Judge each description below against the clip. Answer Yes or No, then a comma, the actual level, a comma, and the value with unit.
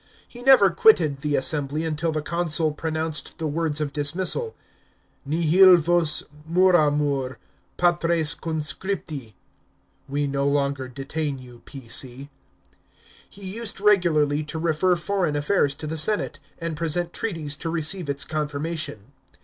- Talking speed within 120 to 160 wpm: Yes, slow, 135 wpm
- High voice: No, medium, 155 Hz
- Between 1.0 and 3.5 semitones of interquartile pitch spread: Yes, average, 3.2 semitones